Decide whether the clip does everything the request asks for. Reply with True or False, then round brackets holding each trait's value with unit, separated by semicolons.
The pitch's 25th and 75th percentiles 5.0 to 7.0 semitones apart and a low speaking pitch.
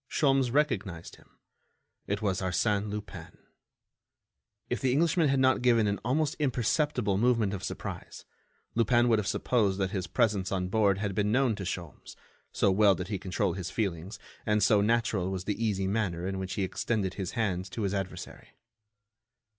False (3.7 semitones; 105 Hz)